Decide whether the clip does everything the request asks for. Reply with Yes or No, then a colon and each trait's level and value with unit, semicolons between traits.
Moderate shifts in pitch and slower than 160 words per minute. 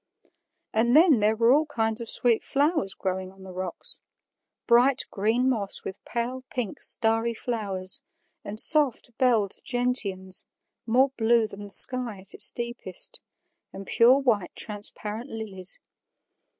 Yes: average, 3.9 semitones; slow, 135 wpm